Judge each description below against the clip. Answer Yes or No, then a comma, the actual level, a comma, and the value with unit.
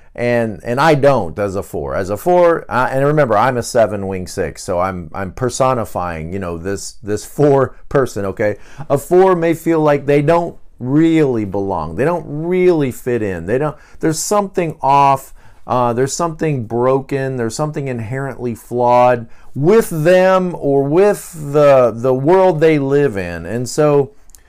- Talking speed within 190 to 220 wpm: No, average, 165 wpm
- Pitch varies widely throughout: Yes, wide, 6.1 semitones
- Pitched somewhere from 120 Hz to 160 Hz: Yes, low, 135 Hz